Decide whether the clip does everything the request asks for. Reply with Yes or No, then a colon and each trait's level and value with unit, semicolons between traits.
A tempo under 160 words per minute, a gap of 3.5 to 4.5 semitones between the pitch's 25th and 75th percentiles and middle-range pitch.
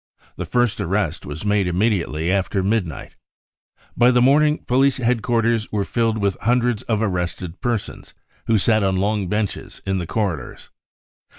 No: average, 150 wpm; average, 3.8 semitones; low, 105 Hz